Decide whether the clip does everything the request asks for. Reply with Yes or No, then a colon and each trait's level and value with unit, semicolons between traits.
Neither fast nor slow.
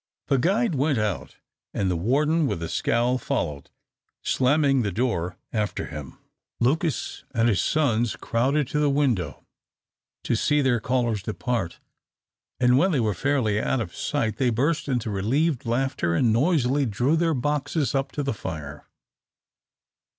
Yes: average, 150 wpm